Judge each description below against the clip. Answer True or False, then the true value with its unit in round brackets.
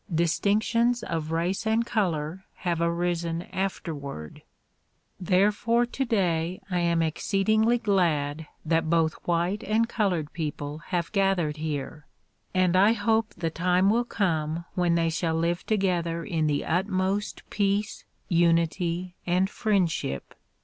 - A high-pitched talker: False (175 Hz)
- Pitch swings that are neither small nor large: True (3.5 semitones)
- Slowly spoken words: True (130 wpm)